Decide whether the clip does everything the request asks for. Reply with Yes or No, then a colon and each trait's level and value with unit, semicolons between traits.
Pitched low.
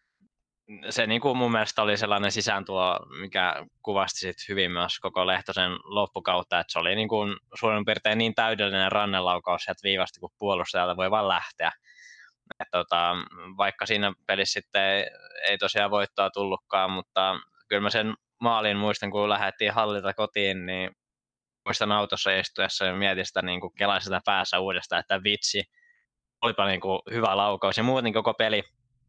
Yes: low, 100 Hz